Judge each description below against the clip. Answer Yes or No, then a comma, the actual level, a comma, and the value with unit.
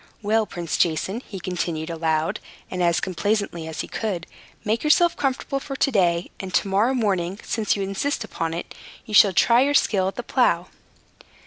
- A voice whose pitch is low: No, high, 195 Hz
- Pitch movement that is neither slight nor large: Yes, average, 4.6 semitones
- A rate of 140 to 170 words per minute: No, average, 185 wpm